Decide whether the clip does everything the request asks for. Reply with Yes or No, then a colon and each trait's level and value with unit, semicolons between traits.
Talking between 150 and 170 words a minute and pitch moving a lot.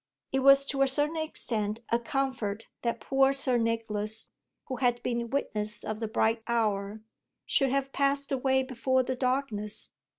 No: average, 160 wpm; average, 3.6 semitones